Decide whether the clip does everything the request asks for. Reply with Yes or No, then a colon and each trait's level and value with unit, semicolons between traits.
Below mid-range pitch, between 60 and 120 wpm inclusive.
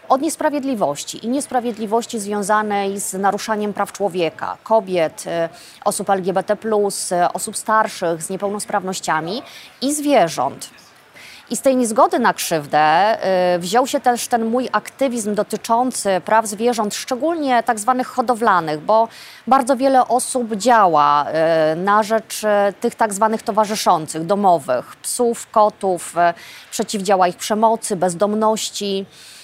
No: high, 215 Hz; slow, 110 wpm